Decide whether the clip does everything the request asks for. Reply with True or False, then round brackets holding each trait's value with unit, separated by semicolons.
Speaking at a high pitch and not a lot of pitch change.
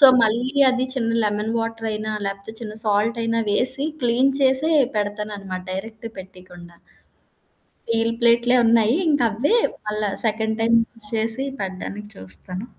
True (220 Hz; 2.2 semitones)